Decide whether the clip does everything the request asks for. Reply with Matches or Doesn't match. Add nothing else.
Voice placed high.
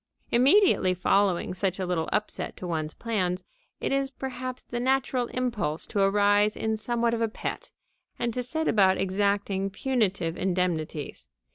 Matches